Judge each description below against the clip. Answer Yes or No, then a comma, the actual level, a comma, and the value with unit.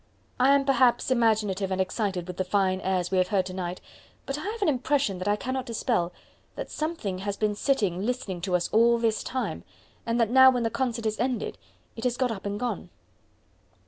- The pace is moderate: No, fast, 210 wpm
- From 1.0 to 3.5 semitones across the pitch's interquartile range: No, average, 5.0 semitones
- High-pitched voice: Yes, high, 220 Hz